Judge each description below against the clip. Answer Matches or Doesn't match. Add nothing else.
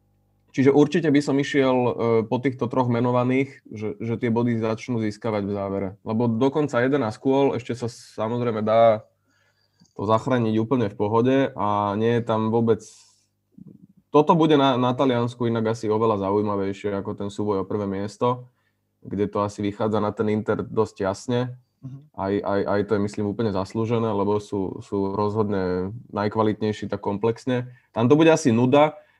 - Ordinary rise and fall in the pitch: Matches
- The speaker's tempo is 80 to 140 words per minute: Doesn't match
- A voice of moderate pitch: Doesn't match